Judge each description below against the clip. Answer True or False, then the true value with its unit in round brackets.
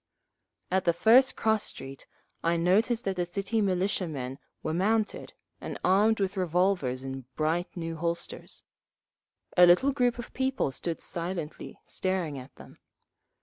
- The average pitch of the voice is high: False (180 Hz)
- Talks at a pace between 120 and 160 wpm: True (140 wpm)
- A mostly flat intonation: False (4.1 semitones)